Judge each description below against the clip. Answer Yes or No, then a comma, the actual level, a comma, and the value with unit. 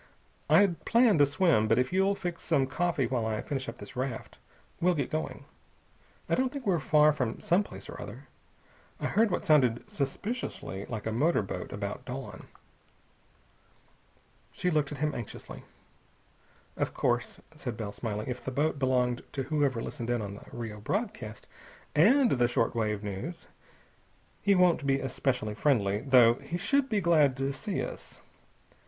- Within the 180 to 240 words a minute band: No, average, 165 wpm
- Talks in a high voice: No, medium, 140 Hz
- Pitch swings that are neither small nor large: No, wide, 6.6 semitones